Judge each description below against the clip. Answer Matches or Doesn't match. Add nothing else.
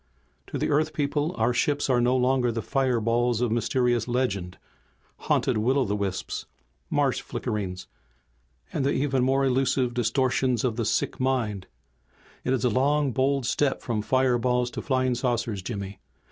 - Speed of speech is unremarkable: Matches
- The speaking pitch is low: Matches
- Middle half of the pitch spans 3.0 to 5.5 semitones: Doesn't match